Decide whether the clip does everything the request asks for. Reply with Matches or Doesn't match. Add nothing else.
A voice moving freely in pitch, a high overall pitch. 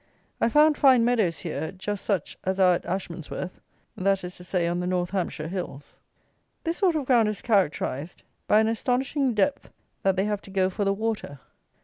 Doesn't match